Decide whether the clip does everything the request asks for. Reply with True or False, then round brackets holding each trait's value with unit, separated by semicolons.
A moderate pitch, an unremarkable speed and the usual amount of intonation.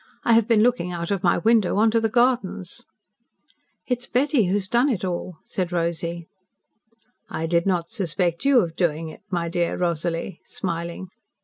True (180 Hz; 180 wpm; 4.9 semitones)